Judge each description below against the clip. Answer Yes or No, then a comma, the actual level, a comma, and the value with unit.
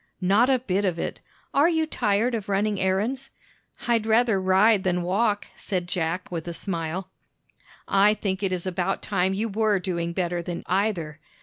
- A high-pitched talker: Yes, high, 195 Hz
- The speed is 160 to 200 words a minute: Yes, average, 175 wpm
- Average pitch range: Yes, average, 3.3 semitones